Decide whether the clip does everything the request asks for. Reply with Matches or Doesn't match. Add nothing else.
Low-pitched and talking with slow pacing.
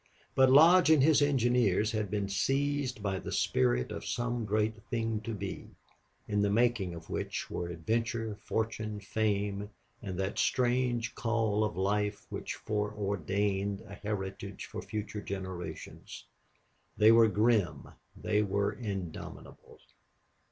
Matches